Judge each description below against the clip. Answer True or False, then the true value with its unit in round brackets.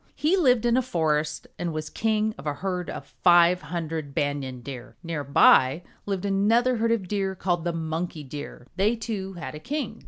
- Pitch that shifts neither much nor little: False (5.9 semitones)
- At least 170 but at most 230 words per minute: True (190 wpm)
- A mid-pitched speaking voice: True (175 Hz)